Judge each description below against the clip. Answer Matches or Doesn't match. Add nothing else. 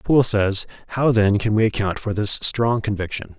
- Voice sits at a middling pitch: Doesn't match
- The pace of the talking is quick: Doesn't match